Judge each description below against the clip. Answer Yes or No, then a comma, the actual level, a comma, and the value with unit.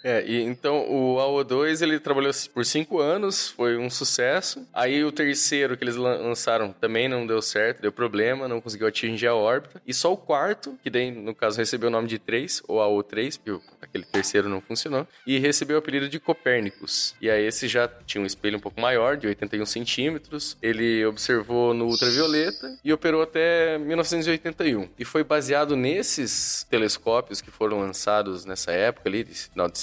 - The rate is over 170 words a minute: Yes, fast, 185 wpm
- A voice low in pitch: Yes, low, 125 Hz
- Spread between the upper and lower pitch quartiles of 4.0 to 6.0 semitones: Yes, average, 4.8 semitones